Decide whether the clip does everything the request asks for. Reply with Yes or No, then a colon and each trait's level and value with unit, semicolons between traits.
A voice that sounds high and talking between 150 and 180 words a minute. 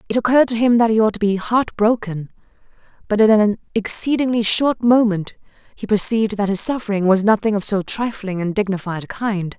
No: high, 210 Hz; average, 195 wpm